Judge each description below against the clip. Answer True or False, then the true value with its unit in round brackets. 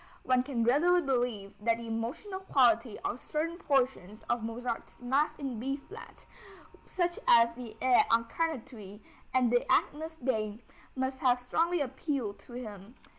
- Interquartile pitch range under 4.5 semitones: True (3.5 semitones)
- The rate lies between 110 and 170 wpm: True (145 wpm)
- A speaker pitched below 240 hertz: False (250 Hz)